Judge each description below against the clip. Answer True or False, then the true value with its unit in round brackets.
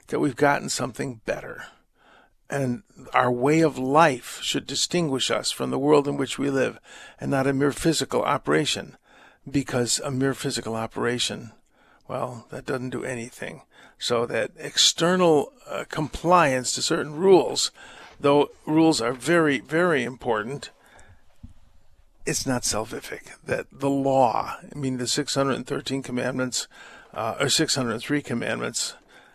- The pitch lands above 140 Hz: False (135 Hz)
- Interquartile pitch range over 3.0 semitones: False (2.7 semitones)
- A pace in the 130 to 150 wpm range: True (135 wpm)